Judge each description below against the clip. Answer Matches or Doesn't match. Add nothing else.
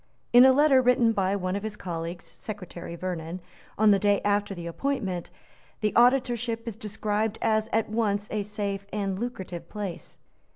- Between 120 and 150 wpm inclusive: Doesn't match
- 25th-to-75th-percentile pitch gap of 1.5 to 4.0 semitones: Matches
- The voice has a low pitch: Doesn't match